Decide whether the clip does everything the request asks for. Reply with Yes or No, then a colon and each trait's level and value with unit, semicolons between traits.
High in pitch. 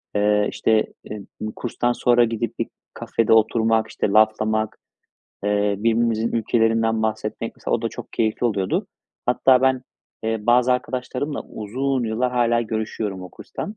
No: low, 115 Hz